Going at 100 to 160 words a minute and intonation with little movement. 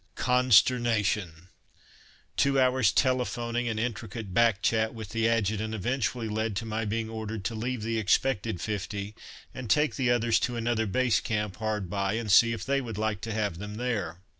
No: average, 175 wpm; narrow, 2.3 semitones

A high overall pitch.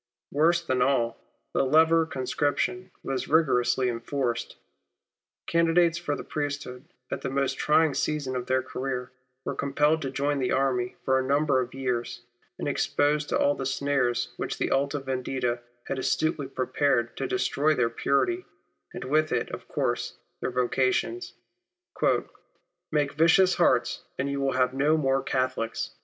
No: low, 135 Hz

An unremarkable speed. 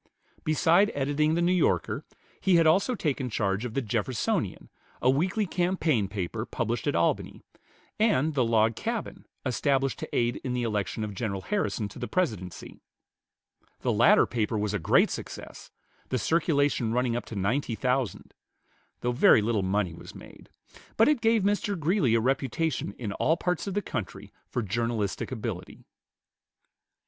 Yes: average, 160 wpm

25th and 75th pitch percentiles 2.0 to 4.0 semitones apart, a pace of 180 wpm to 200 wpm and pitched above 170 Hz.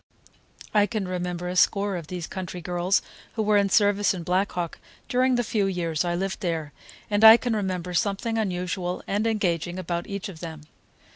Yes: average, 2.7 semitones; average, 190 wpm; medium, 185 Hz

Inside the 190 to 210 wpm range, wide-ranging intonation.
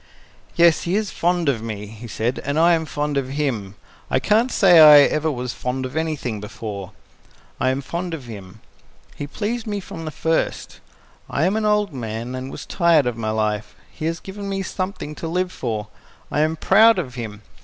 Yes: average, 200 wpm; wide, 6.6 semitones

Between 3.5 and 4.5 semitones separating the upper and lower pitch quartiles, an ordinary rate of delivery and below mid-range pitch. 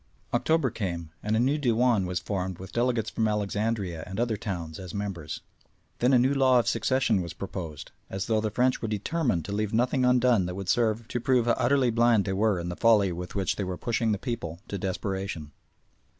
No: average, 4.2 semitones; fast, 210 wpm; low, 105 Hz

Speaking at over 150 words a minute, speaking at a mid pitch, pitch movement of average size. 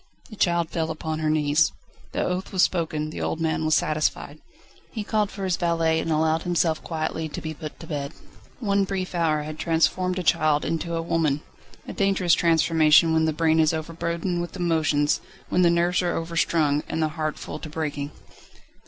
No: average, 190 wpm; medium, 160 Hz; narrow, 1.8 semitones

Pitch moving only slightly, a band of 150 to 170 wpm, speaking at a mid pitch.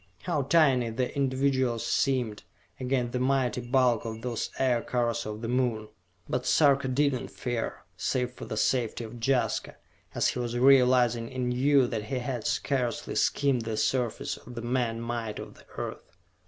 No: narrow, 2.1 semitones; average, 165 wpm; low, 125 Hz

